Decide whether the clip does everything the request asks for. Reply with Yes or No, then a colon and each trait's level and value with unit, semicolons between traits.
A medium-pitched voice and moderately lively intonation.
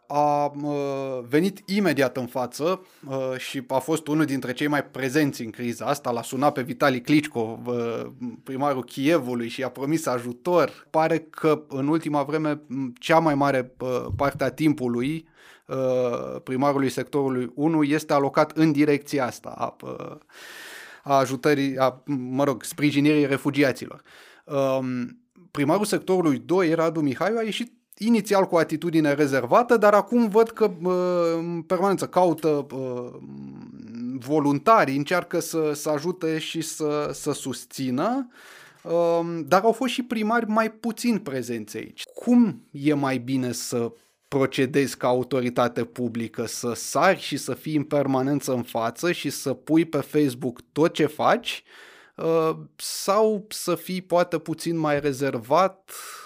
Yes: medium, 145 Hz; average, 4.3 semitones